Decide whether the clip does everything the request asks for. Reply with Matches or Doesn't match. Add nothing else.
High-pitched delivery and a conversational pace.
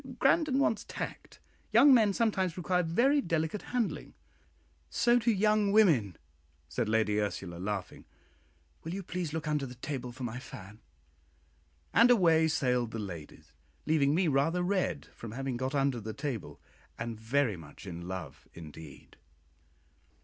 Doesn't match